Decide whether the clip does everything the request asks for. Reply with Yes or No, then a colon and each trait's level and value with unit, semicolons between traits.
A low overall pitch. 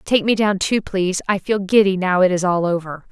No: high, 190 Hz